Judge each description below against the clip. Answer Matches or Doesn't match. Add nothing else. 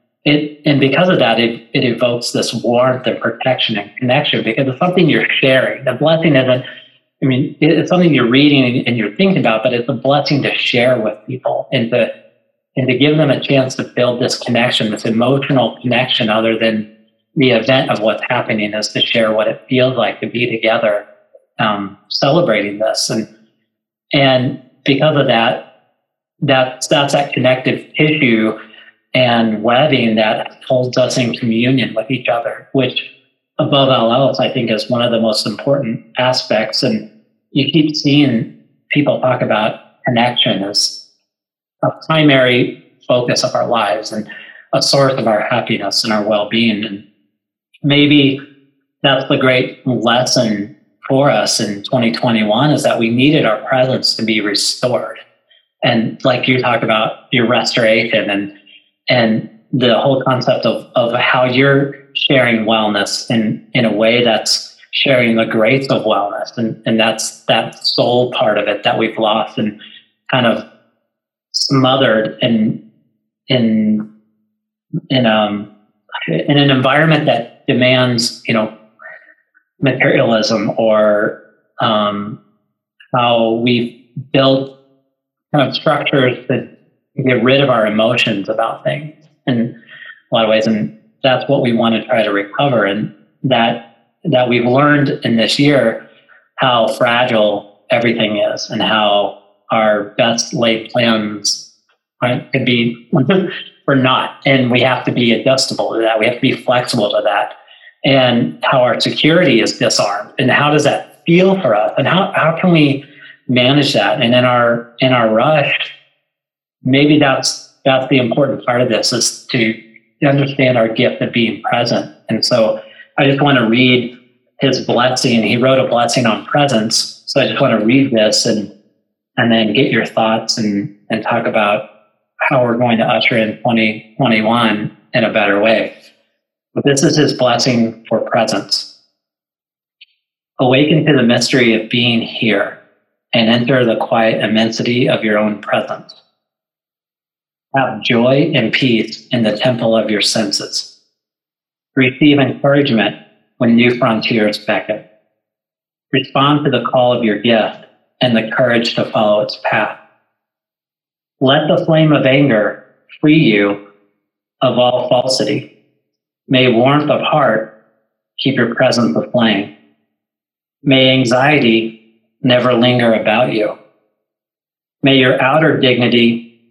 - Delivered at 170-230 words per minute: Doesn't match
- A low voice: Matches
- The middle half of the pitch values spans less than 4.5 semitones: Matches